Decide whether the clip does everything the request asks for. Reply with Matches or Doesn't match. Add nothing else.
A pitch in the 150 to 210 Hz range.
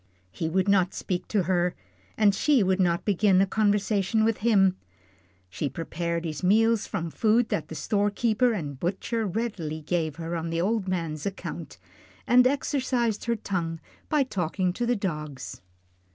Matches